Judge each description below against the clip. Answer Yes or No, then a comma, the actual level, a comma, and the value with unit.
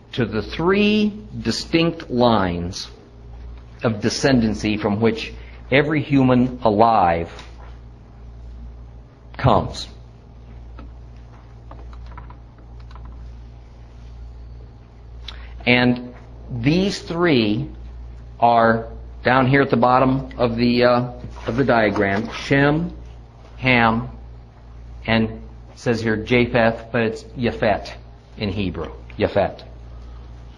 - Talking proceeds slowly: Yes, slow, 80 wpm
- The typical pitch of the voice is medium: No, low, 100 Hz